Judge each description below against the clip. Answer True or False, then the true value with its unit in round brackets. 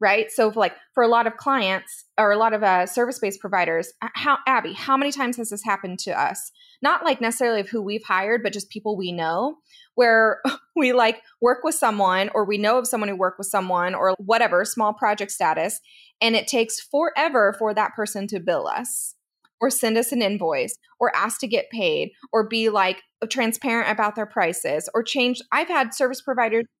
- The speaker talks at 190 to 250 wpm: True (200 wpm)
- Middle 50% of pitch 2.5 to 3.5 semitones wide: False (4.1 semitones)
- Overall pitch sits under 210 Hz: False (225 Hz)